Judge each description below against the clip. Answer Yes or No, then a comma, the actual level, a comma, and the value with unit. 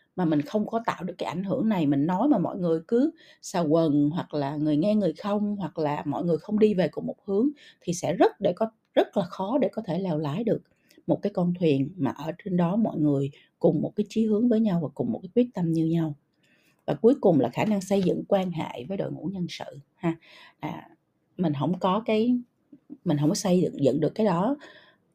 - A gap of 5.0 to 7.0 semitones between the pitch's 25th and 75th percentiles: Yes, average, 5.3 semitones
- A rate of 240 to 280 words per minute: Yes, average, 245 wpm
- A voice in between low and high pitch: Yes, medium, 180 Hz